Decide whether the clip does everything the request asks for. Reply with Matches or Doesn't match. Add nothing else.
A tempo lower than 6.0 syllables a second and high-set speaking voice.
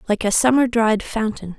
Matches